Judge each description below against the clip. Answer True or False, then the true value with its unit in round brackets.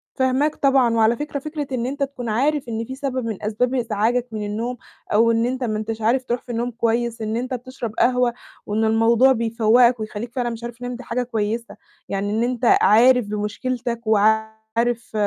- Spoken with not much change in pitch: True (2.3 semitones)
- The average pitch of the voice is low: False (235 Hz)